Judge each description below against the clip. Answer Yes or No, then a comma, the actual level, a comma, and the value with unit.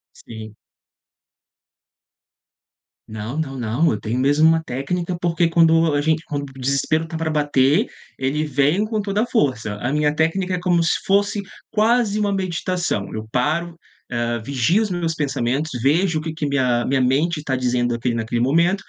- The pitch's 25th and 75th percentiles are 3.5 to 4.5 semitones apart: No, average, 5.0 semitones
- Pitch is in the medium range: Yes, medium, 150 Hz